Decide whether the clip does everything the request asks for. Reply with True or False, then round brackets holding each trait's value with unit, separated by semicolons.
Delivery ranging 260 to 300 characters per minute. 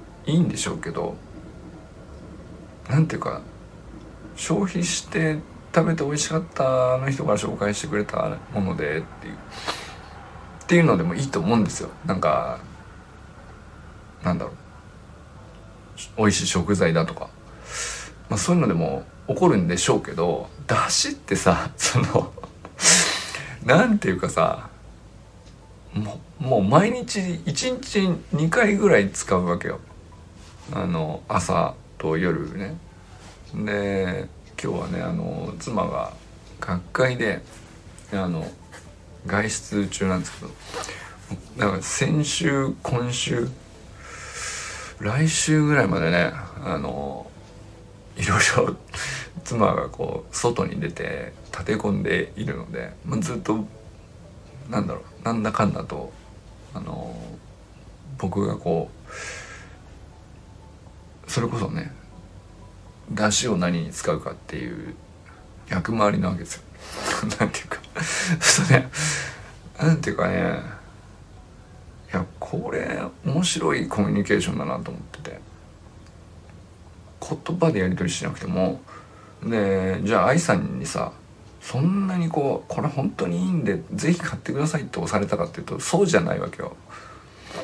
False (235 characters per minute)